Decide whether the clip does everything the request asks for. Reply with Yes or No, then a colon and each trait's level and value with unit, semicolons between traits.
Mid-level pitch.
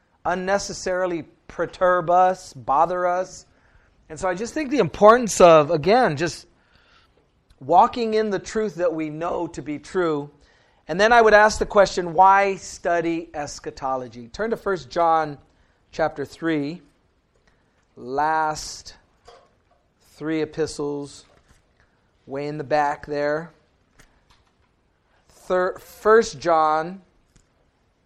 Yes: medium, 165 Hz